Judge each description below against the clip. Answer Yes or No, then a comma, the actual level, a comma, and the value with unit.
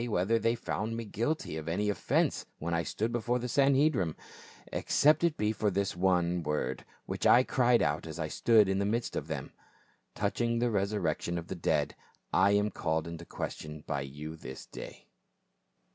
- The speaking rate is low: No, average, 180 wpm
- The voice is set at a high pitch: No, low, 100 Hz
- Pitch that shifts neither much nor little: No, wide, 6.1 semitones